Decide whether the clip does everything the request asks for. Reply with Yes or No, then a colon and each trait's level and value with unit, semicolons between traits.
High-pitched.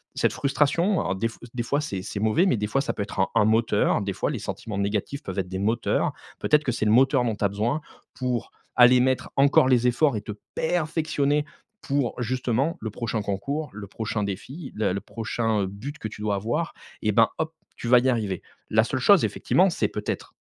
No: low, 120 Hz